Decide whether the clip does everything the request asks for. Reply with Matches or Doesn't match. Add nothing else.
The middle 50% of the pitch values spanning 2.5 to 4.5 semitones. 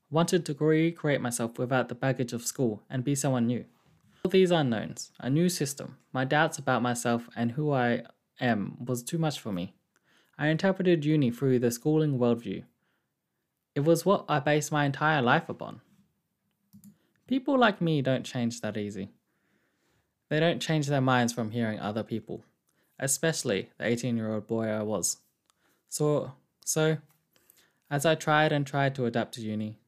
Doesn't match